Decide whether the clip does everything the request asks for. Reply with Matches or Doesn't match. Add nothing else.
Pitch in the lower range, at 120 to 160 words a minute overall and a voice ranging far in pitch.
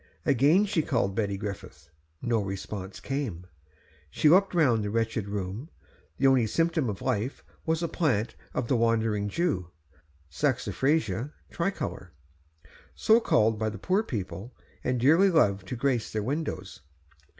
Matches